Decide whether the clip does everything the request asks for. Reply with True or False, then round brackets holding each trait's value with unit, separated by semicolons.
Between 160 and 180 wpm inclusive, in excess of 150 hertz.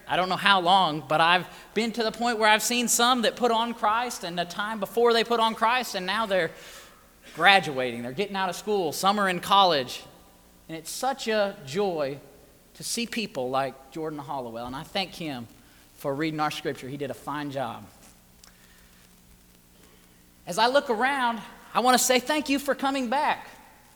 False (195 wpm; 185 Hz)